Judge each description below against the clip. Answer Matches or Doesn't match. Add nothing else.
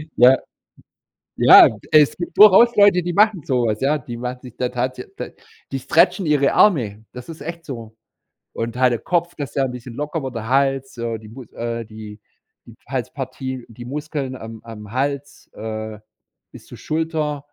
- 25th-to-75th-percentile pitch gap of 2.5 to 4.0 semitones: Doesn't match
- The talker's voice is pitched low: Matches